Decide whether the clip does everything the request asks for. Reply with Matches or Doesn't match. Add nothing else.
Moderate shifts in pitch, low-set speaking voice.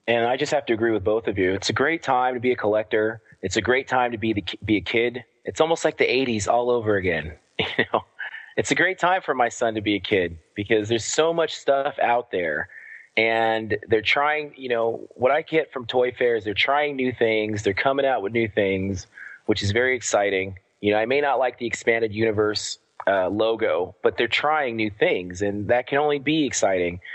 Matches